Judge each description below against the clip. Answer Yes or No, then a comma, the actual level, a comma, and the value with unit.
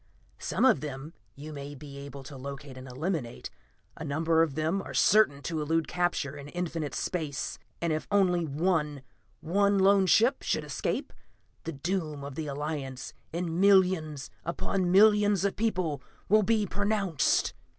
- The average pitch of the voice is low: No, medium, 160 Hz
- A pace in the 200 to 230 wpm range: No, average, 155 wpm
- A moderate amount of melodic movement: Yes, average, 4.9 semitones